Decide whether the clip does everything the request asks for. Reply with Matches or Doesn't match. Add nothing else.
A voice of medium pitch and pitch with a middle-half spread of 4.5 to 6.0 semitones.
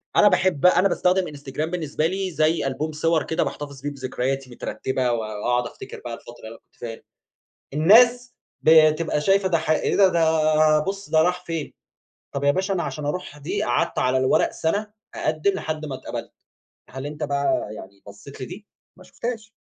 Matches